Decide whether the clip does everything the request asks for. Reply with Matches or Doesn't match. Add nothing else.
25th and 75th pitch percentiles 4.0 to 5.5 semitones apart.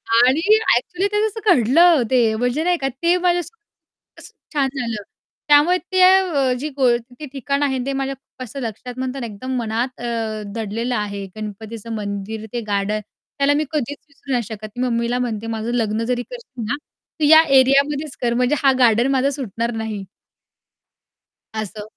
Matches